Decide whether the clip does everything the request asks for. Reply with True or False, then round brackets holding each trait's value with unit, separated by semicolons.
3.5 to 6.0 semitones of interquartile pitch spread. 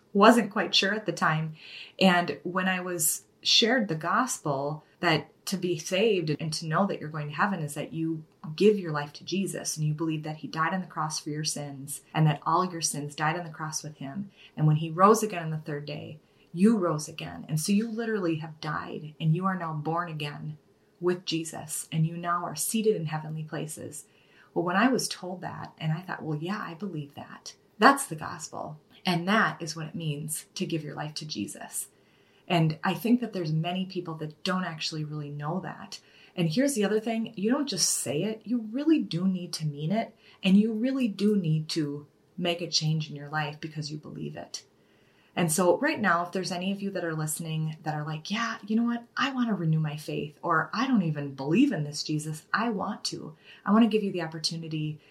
True (4.1 semitones)